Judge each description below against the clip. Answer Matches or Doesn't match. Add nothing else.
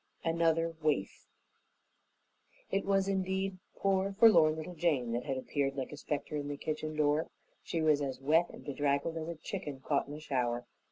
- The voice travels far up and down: Doesn't match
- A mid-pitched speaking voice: Matches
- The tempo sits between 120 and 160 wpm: Doesn't match